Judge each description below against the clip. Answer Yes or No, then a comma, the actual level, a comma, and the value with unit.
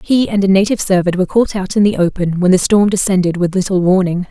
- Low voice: No, high, 190 Hz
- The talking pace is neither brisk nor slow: No, fast, 250 wpm